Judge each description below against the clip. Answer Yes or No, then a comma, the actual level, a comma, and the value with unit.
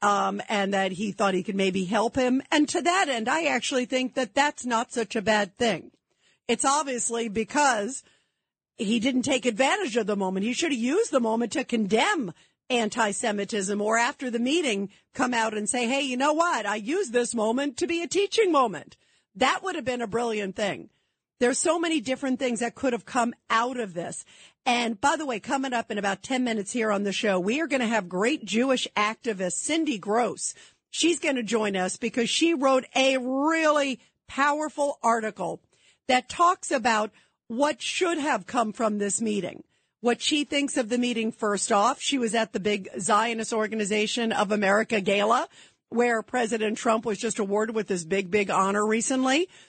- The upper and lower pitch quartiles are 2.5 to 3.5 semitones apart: No, average, 4.2 semitones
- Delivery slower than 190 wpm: No, average, 195 wpm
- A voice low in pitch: No, high, 235 Hz